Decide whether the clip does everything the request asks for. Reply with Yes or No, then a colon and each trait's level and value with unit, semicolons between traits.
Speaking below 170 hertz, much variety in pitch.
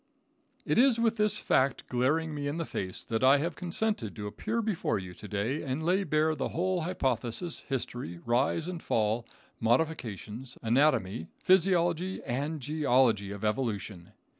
Yes: medium, 140 Hz; wide, 7.0 semitones